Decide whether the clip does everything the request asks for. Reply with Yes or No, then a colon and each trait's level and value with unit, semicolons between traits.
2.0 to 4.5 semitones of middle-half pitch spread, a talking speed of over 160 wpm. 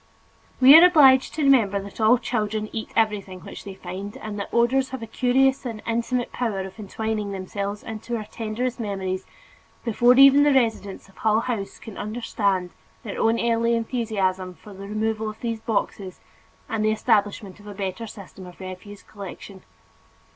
Yes: average, 3.0 semitones; average, 170 wpm